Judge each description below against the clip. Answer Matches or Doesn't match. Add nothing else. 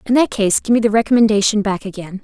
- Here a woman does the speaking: Matches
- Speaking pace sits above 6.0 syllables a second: Matches